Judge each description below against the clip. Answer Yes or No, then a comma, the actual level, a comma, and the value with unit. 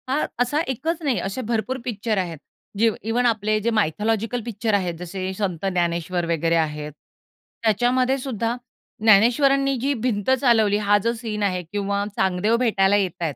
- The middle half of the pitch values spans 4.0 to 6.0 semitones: Yes, average, 4.3 semitones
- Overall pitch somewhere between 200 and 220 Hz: Yes, high, 215 Hz